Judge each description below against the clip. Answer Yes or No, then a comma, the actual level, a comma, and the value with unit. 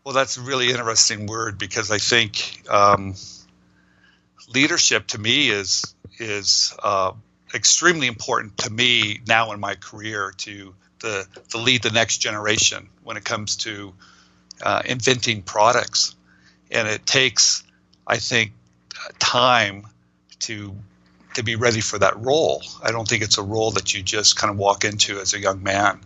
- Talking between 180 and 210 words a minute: No, average, 155 wpm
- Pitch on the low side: Yes, low, 105 Hz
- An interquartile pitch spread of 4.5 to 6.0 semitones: No, average, 3.2 semitones